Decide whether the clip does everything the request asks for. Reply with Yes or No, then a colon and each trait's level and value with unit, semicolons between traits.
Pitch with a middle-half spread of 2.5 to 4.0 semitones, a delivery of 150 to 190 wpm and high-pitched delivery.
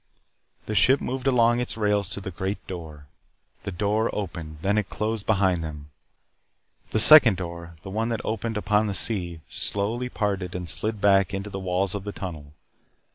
No: average, 3.4 semitones; average, 180 wpm; low, 100 Hz